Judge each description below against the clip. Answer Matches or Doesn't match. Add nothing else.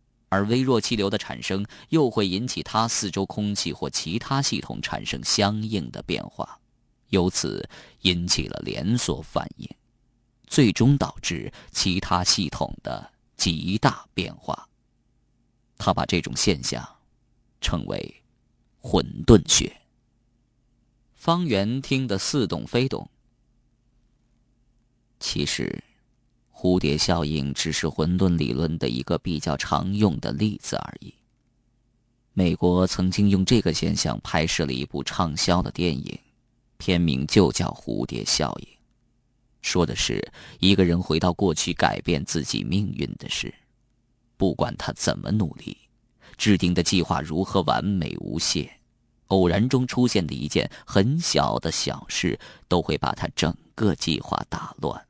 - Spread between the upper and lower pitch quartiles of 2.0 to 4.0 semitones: Doesn't match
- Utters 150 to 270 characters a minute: Matches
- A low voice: Matches